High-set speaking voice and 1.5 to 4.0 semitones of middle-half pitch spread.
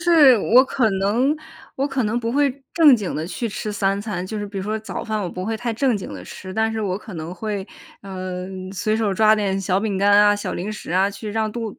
Yes: high, 210 Hz; average, 2.7 semitones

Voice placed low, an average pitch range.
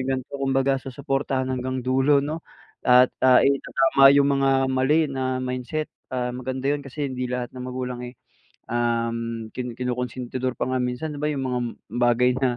No: low, 130 Hz; narrow, 1.5 semitones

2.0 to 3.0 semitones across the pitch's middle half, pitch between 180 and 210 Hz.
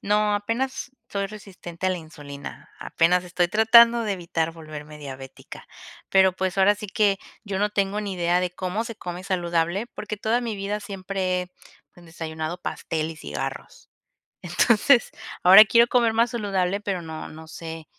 No: average, 3.7 semitones; high, 190 Hz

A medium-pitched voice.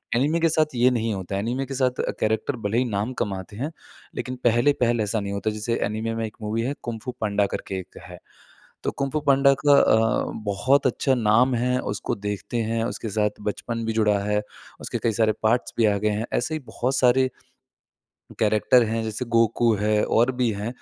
No: low, 115 Hz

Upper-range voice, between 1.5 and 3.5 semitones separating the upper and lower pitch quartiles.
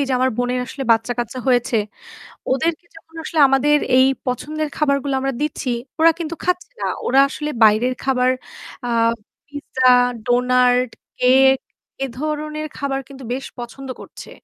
Yes: very high, 270 Hz; average, 3.1 semitones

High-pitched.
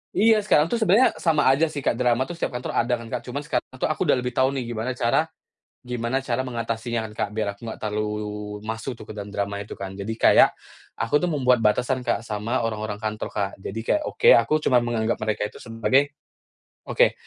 No: low, 120 Hz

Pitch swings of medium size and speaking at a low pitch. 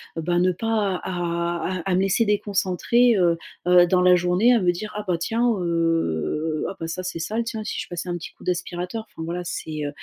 No: average, 3.0 semitones; medium, 180 Hz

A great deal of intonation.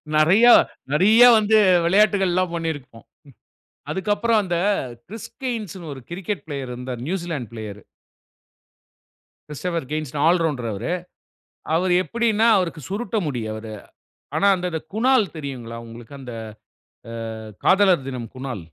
Yes: wide, 7.4 semitones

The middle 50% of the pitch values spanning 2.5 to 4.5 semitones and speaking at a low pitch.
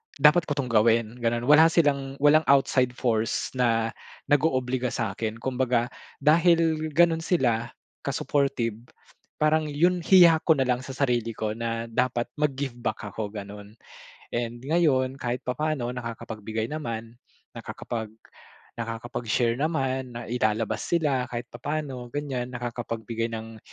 Yes: average, 4.1 semitones; low, 125 Hz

